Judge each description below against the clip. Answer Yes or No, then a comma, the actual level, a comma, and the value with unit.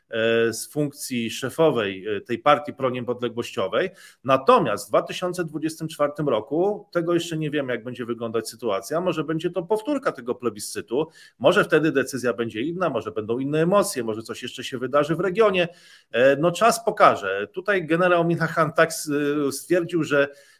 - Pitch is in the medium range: Yes, medium, 150 Hz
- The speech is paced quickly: No, average, 145 wpm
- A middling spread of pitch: No, wide, 5.8 semitones